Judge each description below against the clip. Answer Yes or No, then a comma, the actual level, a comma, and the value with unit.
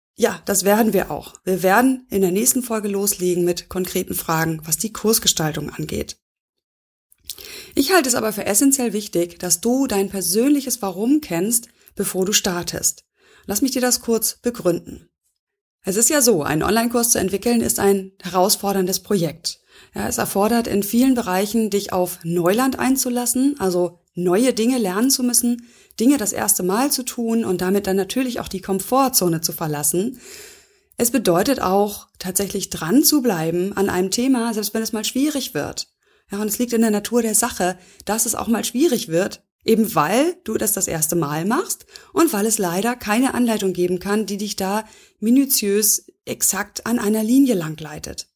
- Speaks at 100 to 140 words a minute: No, average, 170 wpm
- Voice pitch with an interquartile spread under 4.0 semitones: No, average, 4.7 semitones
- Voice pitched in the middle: No, high, 210 Hz